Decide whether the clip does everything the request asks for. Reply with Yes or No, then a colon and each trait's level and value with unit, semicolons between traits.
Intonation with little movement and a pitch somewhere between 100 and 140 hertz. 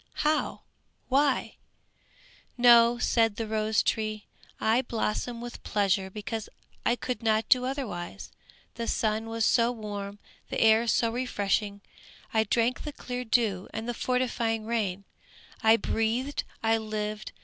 No: narrow, 2.1 semitones; high, 225 Hz